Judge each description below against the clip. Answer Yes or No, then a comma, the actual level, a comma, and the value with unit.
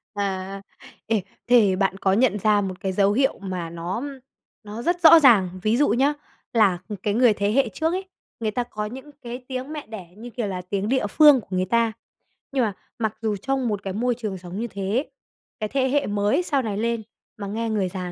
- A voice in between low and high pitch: No, high, 215 Hz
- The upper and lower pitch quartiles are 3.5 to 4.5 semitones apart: Yes, average, 4.2 semitones